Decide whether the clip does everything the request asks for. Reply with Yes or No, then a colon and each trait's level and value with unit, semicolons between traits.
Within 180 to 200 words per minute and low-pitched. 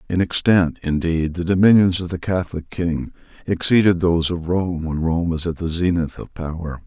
Yes: average, 185 wpm; very low, 85 Hz